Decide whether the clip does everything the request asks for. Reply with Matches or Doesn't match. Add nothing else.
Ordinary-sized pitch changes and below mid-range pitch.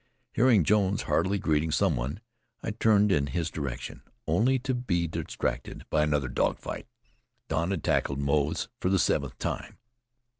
Doesn't match